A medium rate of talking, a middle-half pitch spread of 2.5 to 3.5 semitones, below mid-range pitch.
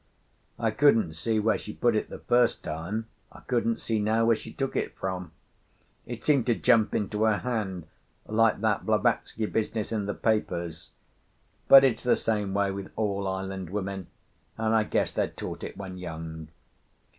Yes: average, 175 wpm; average, 2.9 semitones; low, 105 Hz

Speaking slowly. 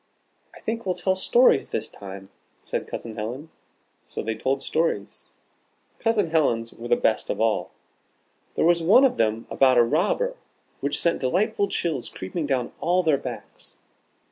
No: average, 160 wpm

